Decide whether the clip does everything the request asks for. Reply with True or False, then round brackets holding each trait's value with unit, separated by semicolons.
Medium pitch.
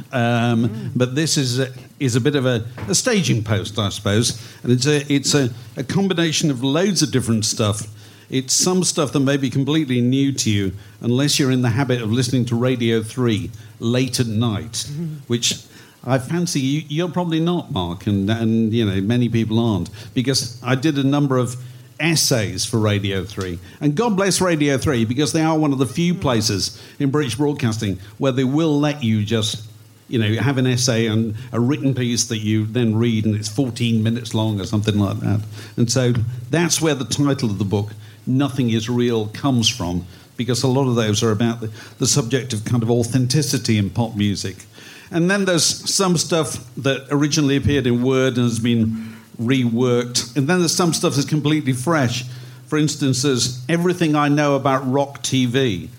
False (125 Hz)